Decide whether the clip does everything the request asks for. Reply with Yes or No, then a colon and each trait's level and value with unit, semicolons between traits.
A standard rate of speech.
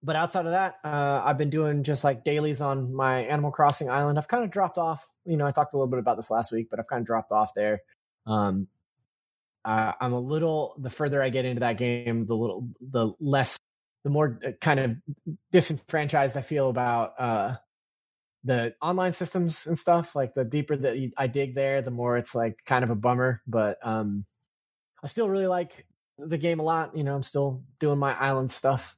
No: fast, 210 wpm